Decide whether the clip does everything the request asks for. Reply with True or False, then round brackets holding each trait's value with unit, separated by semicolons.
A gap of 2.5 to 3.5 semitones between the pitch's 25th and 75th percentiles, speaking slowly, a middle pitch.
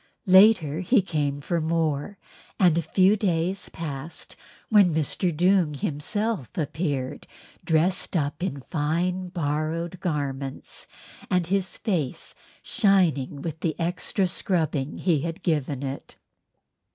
False (3.9 semitones; 115 wpm; 165 Hz)